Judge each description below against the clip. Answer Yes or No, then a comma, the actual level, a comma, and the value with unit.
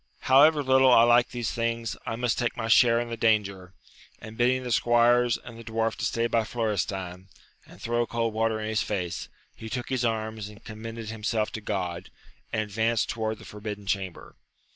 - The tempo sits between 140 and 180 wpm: No, average, 190 wpm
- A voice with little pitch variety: Yes, narrow, 1.8 semitones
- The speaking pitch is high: No, low, 115 Hz